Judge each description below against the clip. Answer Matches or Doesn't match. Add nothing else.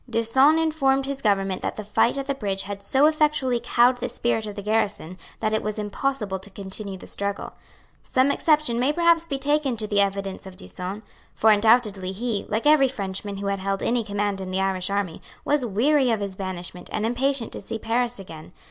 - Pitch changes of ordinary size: Matches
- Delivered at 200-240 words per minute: Matches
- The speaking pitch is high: Matches